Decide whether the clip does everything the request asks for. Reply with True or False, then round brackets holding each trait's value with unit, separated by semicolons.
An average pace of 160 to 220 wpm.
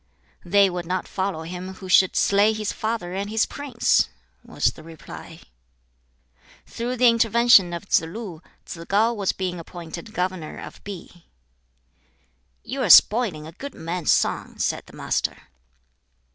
False (145 wpm)